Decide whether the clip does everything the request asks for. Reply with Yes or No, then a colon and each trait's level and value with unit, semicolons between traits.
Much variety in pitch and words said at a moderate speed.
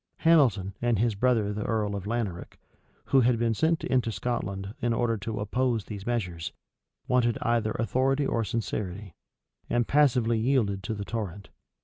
No: average, 3.1 semitones; average, 155 wpm